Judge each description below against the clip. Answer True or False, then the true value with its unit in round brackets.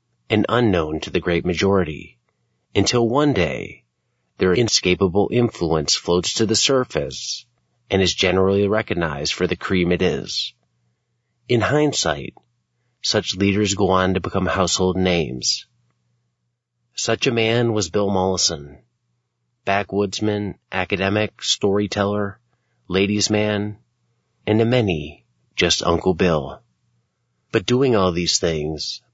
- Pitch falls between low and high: False (95 Hz)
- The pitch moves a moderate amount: True (4.7 semitones)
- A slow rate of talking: True (115 wpm)